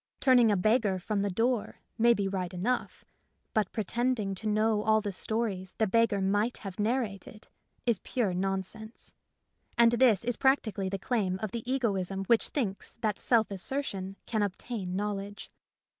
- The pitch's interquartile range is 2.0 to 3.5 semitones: Yes, average, 3.2 semitones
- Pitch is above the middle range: Yes, high, 210 Hz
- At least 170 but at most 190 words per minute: No, average, 160 wpm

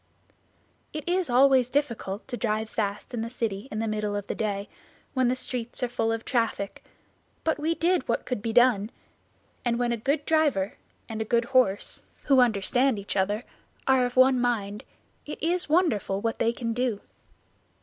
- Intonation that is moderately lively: Yes, average, 3.5 semitones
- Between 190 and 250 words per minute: No, average, 180 wpm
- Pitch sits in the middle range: No, high, 240 Hz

